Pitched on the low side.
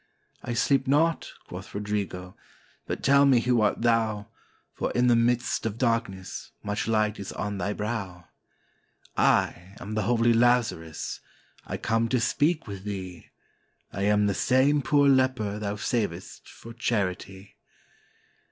Yes: low, 110 Hz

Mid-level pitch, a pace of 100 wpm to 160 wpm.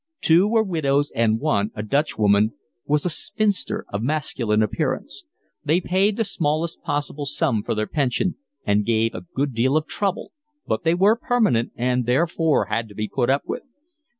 No: medium, 145 Hz; average, 175 wpm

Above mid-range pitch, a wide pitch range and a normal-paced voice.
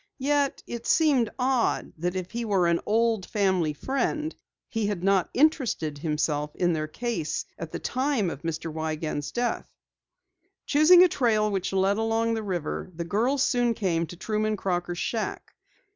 Yes: high, 205 Hz; wide, 5.9 semitones; average, 160 wpm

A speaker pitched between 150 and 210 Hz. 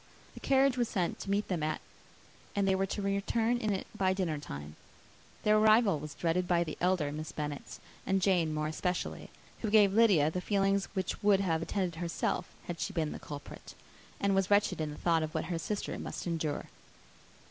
Yes: medium, 185 Hz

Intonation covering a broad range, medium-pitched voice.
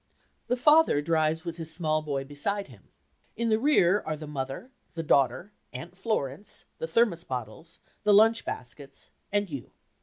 Yes: wide, 6.3 semitones; medium, 165 Hz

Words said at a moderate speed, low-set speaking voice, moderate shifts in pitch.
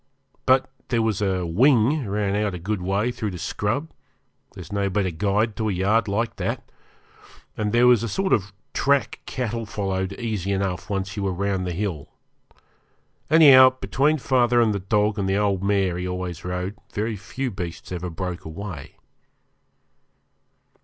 Yes: average, 165 wpm; low, 100 Hz; average, 3.6 semitones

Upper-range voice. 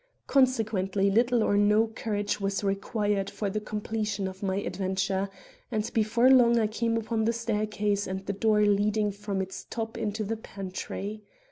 Yes: high, 210 Hz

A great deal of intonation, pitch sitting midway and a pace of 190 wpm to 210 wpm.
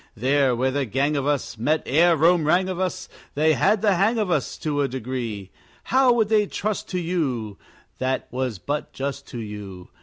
Yes: wide, 5.9 semitones; medium, 145 Hz; average, 195 wpm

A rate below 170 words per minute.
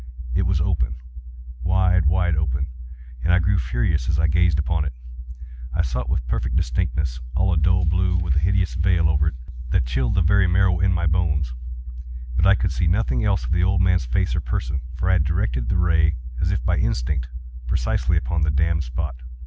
No: average, 195 wpm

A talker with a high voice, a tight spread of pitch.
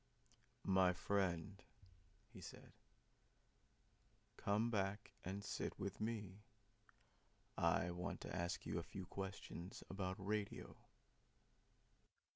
No: very low, 95 Hz; narrow, 1.8 semitones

